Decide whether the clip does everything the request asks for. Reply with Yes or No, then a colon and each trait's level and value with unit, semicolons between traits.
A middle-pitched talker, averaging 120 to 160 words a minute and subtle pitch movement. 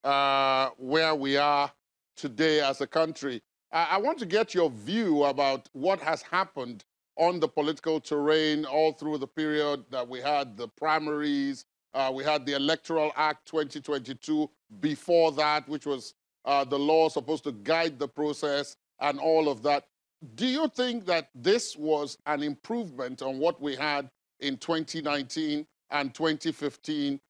Yes: medium, 150 Hz; average, 155 wpm; narrow, 2.2 semitones